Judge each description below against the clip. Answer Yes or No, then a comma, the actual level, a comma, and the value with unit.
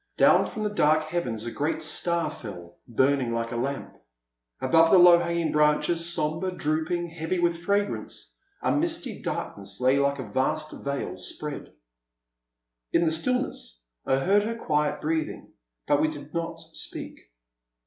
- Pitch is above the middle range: No, medium, 155 Hz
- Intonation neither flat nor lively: Yes, average, 3.6 semitones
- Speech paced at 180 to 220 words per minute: No, average, 150 wpm